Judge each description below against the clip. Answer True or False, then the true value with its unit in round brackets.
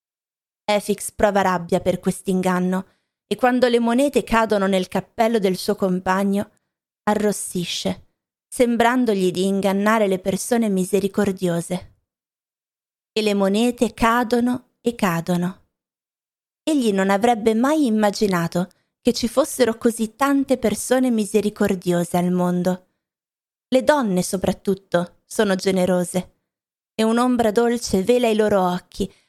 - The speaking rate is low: True (110 wpm)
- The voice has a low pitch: False (205 Hz)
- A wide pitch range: False (4.0 semitones)